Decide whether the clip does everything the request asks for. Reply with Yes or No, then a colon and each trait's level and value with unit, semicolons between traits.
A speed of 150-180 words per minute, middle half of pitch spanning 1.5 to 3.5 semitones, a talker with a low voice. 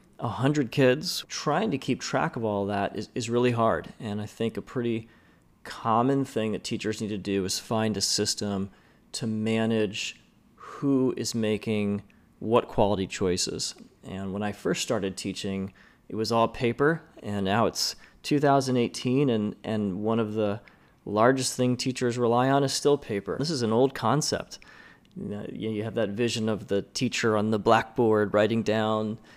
Yes: average, 170 wpm; average, 2.9 semitones; low, 110 Hz